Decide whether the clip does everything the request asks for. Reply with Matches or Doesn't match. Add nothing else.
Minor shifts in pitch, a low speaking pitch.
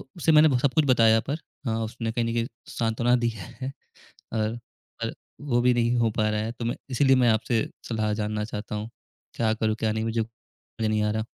Matches